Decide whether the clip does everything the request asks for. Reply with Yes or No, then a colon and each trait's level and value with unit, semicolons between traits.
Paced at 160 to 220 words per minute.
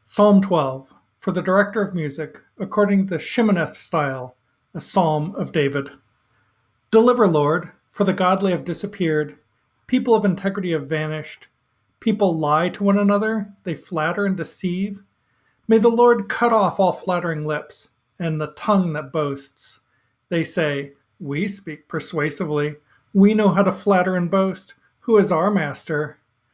No: average, 150 wpm